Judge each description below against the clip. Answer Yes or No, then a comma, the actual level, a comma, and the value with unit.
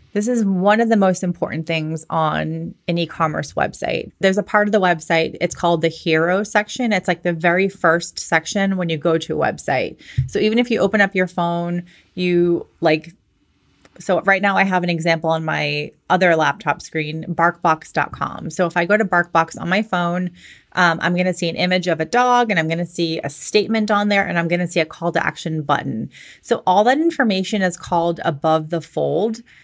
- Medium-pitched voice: Yes, medium, 175 Hz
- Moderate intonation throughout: Yes, average, 3.1 semitones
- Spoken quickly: Yes, fast, 210 wpm